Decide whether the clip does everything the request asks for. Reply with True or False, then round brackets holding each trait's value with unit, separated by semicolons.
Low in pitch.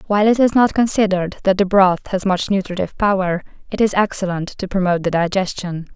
False (190 Hz)